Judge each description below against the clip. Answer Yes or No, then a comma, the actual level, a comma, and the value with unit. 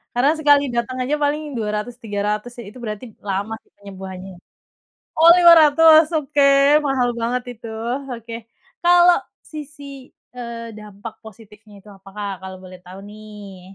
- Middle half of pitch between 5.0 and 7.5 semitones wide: Yes, wide, 5.6 semitones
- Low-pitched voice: No, high, 230 Hz